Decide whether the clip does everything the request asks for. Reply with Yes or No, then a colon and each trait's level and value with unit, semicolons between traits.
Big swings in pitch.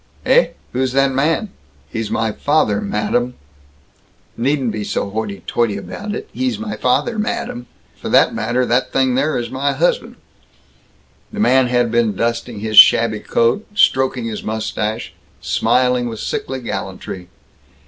No: average, 3.6 semitones